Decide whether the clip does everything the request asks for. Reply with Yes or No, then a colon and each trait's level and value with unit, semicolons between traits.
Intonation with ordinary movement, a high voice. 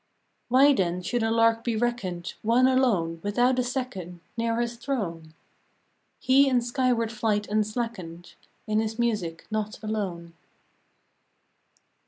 Yes: average, 4.4 semitones; high, 225 Hz